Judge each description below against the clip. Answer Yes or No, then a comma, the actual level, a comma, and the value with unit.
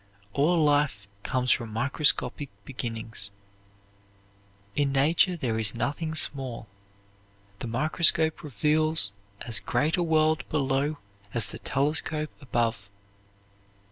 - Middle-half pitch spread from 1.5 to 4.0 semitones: No, average, 5.0 semitones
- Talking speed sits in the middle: No, slow, 105 wpm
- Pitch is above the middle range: No, medium, 140 Hz